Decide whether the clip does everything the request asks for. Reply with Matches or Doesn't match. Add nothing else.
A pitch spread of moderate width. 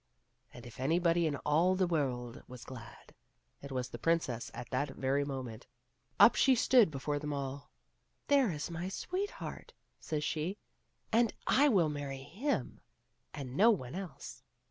Doesn't match